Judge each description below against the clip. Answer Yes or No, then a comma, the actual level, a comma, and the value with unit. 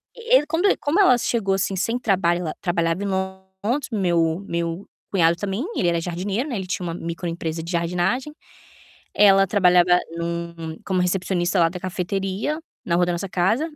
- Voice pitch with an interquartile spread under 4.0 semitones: Yes, average, 2.9 semitones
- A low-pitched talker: No, medium, 185 Hz